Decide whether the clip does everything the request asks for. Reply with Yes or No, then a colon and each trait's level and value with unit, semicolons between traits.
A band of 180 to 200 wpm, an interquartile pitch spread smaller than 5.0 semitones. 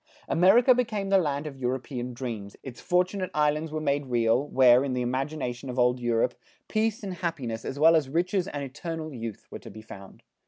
No: average, 195 wpm; wide, 5.5 semitones